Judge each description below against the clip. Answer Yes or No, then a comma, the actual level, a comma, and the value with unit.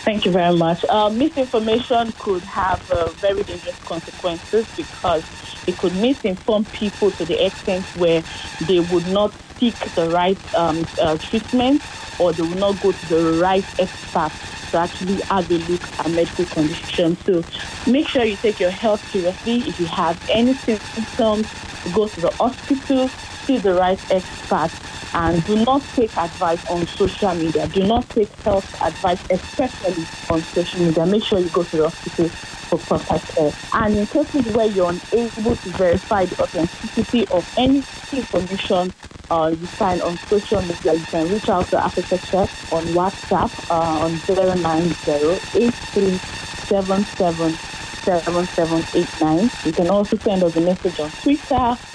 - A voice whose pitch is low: No, medium, 185 Hz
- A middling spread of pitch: Yes, average, 4.3 semitones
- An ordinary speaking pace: Yes, average, 165 wpm